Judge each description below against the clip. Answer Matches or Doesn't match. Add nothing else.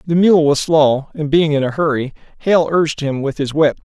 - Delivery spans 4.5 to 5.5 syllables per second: Matches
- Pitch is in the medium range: Matches